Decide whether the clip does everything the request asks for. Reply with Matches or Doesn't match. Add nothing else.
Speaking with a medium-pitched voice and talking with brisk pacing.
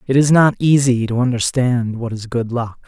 Doesn't match